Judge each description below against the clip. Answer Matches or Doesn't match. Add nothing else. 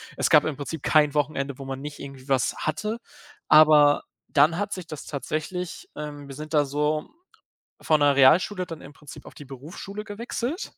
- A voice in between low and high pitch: Matches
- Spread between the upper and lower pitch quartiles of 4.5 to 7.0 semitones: Doesn't match